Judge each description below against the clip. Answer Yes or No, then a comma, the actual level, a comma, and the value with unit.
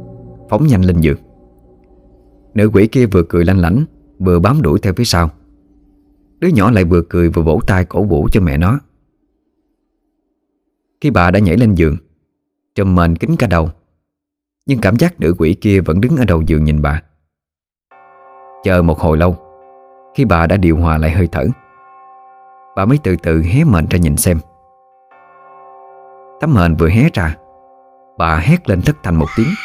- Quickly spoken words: No, average, 175 wpm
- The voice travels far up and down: Yes, wide, 7.9 semitones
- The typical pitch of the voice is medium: No, very low, 90 Hz